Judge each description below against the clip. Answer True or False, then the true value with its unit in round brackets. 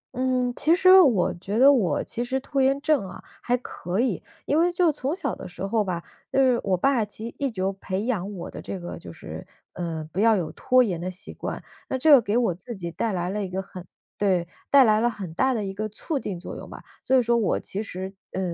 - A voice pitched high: True (215 Hz)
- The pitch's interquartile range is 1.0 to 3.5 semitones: False (5.6 semitones)